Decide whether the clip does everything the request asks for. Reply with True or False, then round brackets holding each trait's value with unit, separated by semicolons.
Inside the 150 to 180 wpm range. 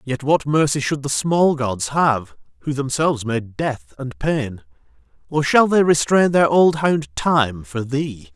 True (170 wpm)